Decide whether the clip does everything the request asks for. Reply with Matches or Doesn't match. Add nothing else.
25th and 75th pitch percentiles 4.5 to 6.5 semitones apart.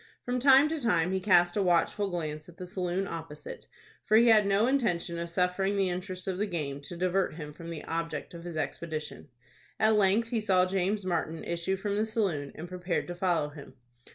Doesn't match